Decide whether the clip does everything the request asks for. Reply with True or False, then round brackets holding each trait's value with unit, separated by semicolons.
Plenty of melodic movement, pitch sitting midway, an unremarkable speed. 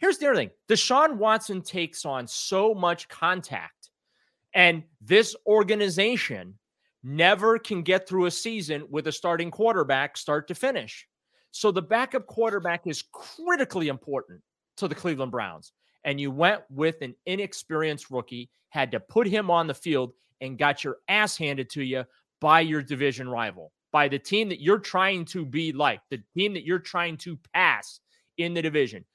True (6.3 semitones; 170 Hz; 170 wpm)